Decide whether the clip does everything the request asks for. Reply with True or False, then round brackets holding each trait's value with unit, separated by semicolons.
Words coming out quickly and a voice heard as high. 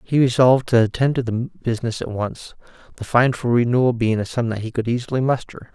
False (220 wpm; 120 Hz)